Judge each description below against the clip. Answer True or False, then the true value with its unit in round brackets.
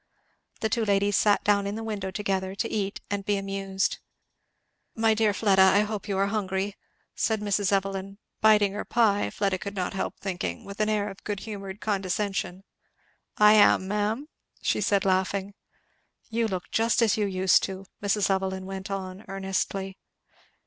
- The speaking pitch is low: False (200 Hz)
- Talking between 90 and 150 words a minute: False (170 wpm)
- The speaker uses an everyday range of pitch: False (1.6 semitones)